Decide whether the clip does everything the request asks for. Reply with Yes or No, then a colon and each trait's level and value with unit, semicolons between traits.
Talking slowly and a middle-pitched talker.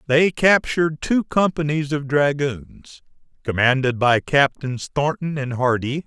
Yes: slow, 120 wpm; medium, 145 Hz